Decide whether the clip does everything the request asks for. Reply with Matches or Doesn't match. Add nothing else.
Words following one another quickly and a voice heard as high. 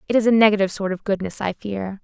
Matches